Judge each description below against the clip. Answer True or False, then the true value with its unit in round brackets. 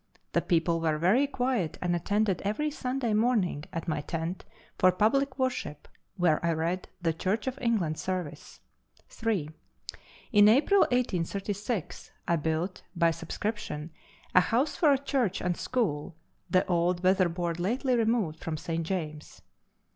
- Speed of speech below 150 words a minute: True (140 wpm)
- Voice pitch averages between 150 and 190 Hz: True (185 Hz)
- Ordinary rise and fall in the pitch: False (5.8 semitones)